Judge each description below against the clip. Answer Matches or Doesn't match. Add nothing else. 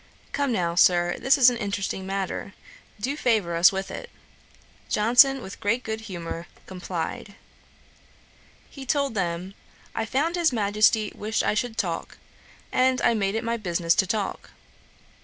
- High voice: Matches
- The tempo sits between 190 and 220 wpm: Doesn't match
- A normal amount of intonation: Matches